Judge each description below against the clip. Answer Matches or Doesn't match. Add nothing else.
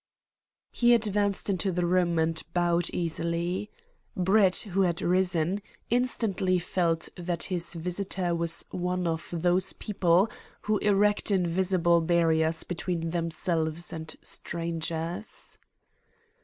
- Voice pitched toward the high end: Doesn't match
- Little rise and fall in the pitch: Matches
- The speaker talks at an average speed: Doesn't match